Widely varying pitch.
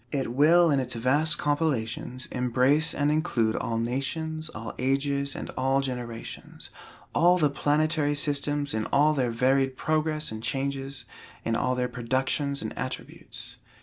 No: average, 3.0 semitones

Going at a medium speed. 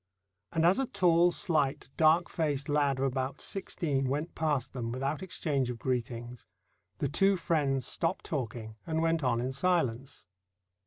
Yes: average, 155 wpm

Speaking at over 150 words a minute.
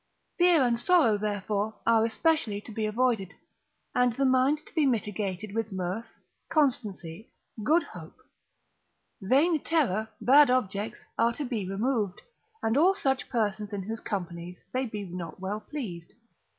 No: average, 145 wpm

